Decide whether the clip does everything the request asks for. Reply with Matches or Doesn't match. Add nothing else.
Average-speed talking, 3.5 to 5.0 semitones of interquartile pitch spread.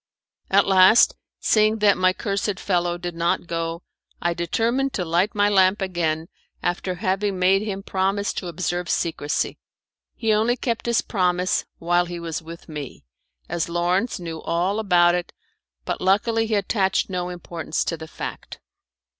Doesn't match